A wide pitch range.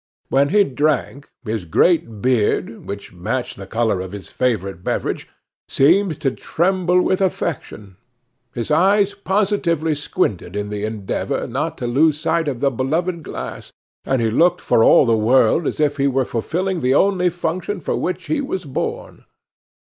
Yes: wide, 7.7 semitones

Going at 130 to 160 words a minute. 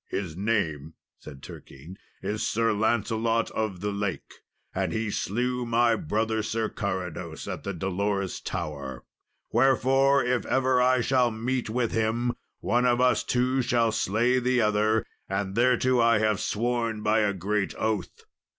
Yes: average, 150 wpm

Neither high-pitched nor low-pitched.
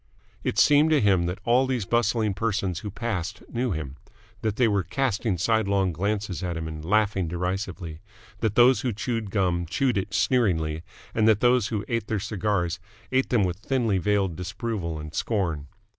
No: low, 100 Hz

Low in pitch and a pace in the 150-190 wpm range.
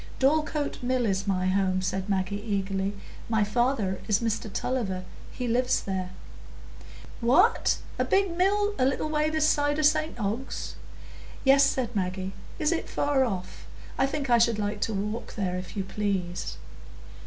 No: high, 225 Hz; average, 160 wpm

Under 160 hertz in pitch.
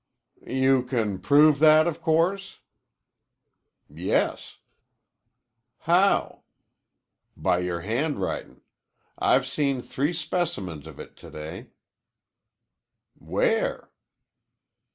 Yes: medium, 140 Hz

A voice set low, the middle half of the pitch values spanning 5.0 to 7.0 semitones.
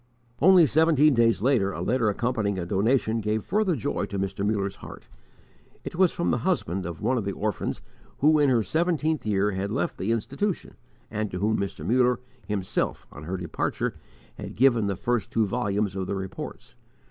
Yes: low, 110 Hz; wide, 5.5 semitones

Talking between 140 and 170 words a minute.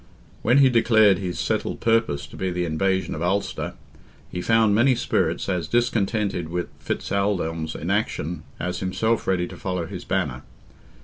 Yes: average, 160 wpm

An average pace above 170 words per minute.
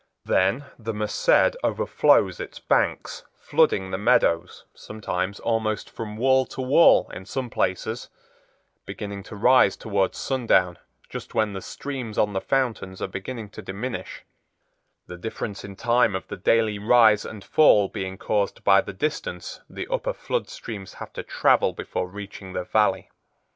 No: average, 155 wpm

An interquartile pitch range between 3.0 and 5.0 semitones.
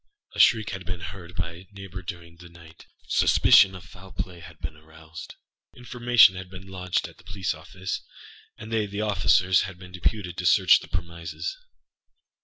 No: narrow, 2.4 semitones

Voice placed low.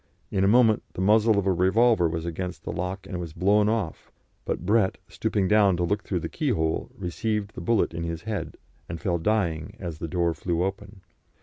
Yes: very low, 95 Hz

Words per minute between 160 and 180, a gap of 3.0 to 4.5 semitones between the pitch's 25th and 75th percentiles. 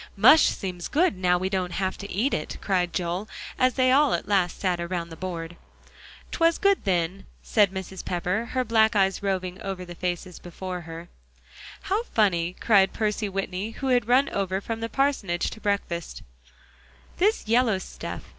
Yes: average, 175 wpm; average, 4.0 semitones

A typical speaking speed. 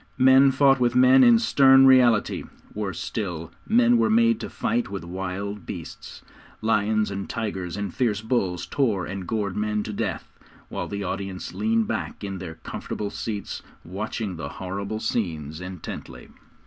Yes: average, 155 wpm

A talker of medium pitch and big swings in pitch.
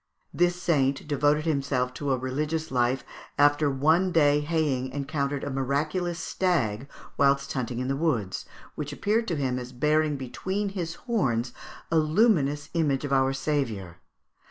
No: medium, 145 Hz; average, 3.3 semitones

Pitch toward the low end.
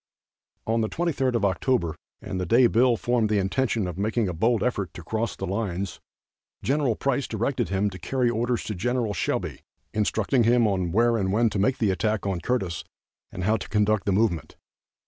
Yes: low, 110 Hz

